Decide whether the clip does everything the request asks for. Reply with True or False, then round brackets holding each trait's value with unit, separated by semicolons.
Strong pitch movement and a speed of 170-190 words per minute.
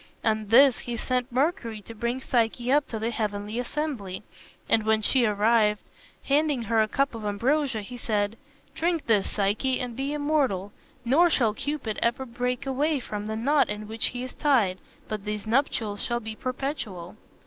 False (4.0 semitones; 175 wpm)